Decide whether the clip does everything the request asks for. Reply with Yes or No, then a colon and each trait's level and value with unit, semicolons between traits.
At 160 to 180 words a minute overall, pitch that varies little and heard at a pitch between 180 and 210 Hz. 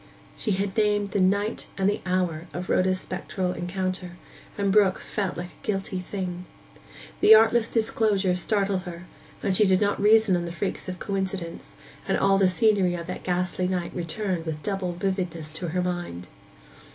Yes: average, 170 wpm; narrow, 2.1 semitones; medium, 185 Hz